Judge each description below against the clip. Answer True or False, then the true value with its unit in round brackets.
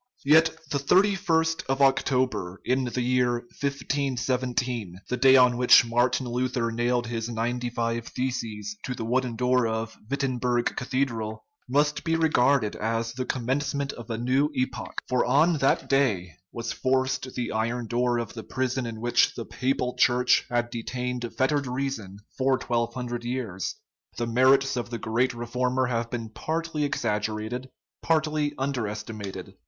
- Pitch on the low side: True (125 Hz)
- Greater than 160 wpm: False (155 wpm)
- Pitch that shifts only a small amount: True (2.2 semitones)